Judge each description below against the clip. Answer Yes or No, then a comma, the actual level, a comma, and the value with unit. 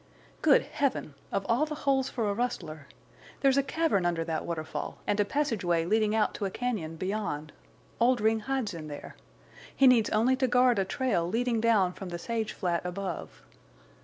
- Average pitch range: No, wide, 6.1 semitones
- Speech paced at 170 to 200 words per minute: Yes, average, 180 wpm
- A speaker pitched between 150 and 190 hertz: No, high, 215 Hz